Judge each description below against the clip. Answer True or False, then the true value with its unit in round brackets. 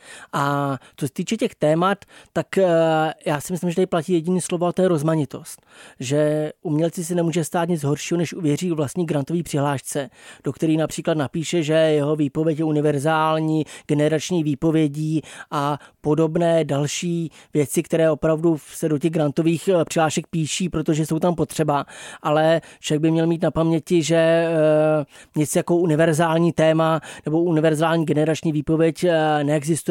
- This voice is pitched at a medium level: True (160 Hz)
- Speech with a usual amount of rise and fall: False (1.9 semitones)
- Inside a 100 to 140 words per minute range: False (155 wpm)